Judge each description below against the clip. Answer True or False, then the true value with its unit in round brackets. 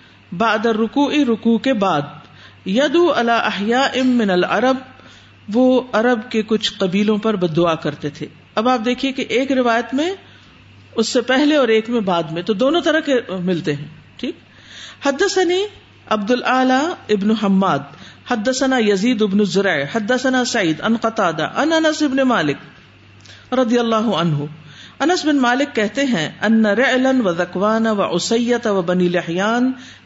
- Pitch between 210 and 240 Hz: True (230 Hz)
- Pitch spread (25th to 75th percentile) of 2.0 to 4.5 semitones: False (5.3 semitones)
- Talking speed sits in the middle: True (145 wpm)